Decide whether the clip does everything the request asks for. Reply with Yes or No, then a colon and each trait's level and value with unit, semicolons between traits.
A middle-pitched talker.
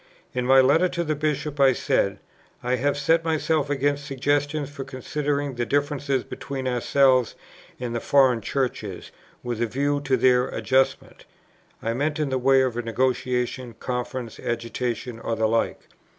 No: low, 130 Hz